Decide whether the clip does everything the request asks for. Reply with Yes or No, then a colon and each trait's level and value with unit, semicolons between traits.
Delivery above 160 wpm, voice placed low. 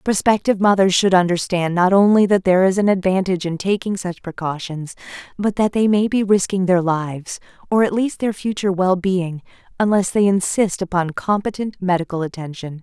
No: average, 170 wpm; high, 190 Hz